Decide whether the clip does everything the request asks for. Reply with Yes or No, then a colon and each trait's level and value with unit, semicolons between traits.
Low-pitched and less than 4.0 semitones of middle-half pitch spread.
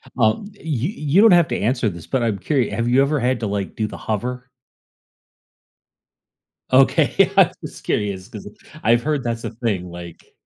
No: low, 120 Hz; average, 4.8 semitones